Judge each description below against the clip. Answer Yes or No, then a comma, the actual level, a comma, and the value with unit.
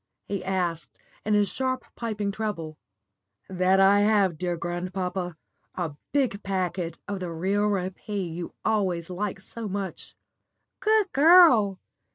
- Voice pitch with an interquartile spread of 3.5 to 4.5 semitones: No, average, 2.8 semitones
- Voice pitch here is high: Yes, high, 195 Hz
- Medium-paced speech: No, slow, 130 wpm